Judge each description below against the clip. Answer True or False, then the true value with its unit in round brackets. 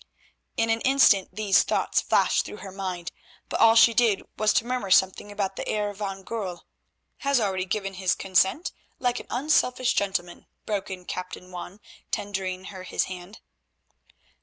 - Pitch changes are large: False (3.2 semitones)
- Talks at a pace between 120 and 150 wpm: False (160 wpm)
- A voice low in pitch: False (200 Hz)